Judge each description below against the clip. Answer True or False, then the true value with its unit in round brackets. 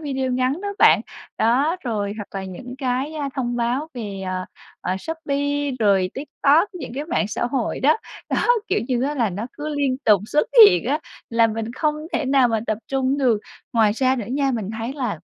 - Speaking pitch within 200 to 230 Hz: False (255 Hz)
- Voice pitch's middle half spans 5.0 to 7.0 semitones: False (4.4 semitones)